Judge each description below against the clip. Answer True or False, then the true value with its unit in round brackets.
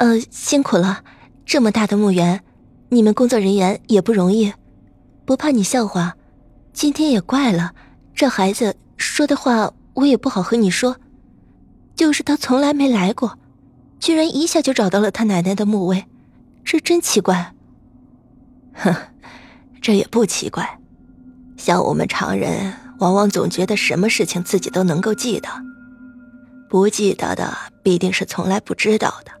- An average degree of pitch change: True (4.8 semitones)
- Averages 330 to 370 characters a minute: False (220 characters per minute)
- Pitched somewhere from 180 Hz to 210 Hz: False (220 Hz)